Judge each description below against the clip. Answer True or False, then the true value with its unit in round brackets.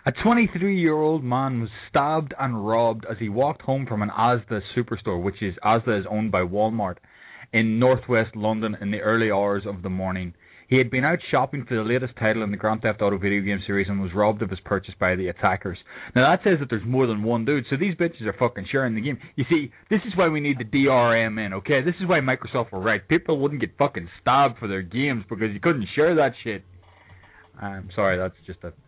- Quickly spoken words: True (235 wpm)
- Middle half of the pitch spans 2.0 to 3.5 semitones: False (5.1 semitones)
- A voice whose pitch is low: True (110 Hz)